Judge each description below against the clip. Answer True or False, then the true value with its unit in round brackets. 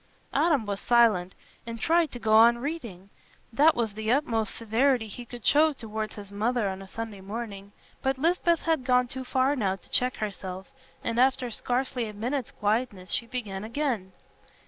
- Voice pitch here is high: True (230 Hz)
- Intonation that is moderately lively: True (3.9 semitones)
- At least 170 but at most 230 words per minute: True (175 wpm)